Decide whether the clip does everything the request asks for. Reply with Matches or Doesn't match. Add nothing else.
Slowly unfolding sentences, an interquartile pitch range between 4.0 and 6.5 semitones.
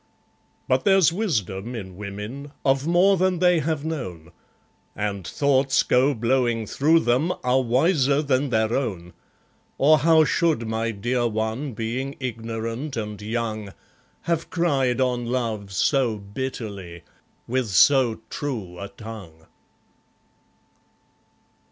Matches